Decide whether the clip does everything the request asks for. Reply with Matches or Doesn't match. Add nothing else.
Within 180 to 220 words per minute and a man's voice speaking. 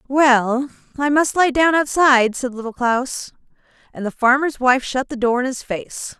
Doesn't match